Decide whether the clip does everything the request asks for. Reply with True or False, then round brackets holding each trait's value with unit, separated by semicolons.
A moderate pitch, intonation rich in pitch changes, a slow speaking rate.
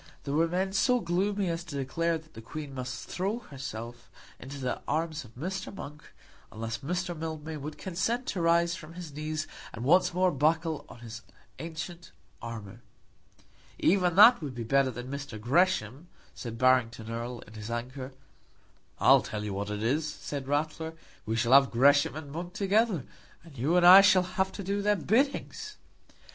False (155 Hz; 5.9 semitones; 175 wpm)